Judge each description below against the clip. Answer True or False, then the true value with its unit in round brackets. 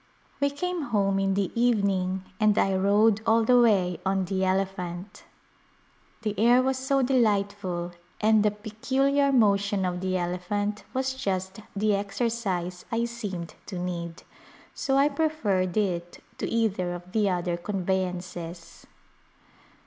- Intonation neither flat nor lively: True (3.8 semitones)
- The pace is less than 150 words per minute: True (135 wpm)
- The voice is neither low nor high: False (200 Hz)